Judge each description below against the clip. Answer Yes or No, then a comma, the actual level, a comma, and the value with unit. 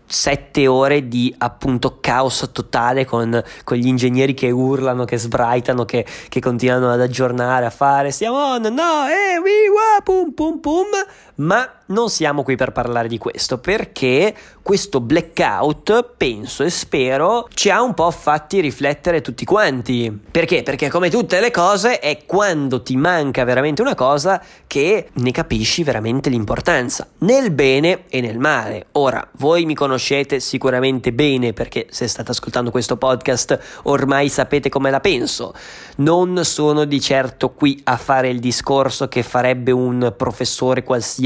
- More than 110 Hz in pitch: Yes, low, 135 Hz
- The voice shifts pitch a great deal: No, average, 4.7 semitones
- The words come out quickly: No, average, 155 wpm